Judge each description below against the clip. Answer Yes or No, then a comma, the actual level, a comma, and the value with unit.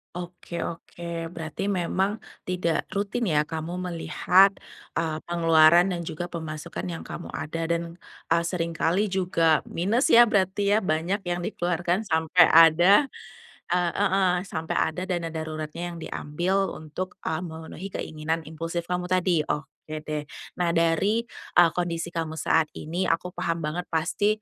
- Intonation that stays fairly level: Yes, narrow, 2.2 semitones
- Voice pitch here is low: No, medium, 170 Hz